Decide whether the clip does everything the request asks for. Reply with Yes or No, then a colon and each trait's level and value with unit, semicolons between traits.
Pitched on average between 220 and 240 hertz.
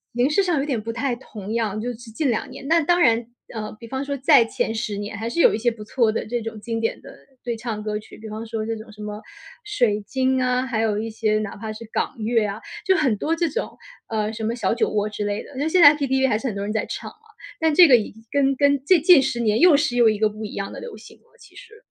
Yes: high, 230 Hz